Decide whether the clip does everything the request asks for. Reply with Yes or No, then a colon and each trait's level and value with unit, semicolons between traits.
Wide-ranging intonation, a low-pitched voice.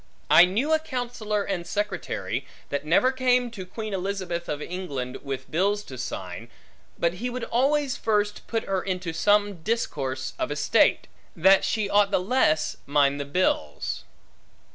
No: wide, 6.7 semitones; high, 190 Hz